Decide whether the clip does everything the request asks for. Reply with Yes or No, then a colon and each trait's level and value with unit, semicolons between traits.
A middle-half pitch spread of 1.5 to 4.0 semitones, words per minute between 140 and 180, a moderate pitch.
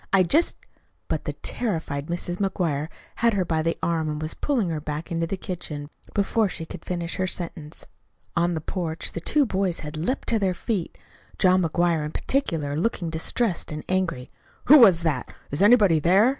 No: average, 3.6 semitones; average, 190 wpm; medium, 170 Hz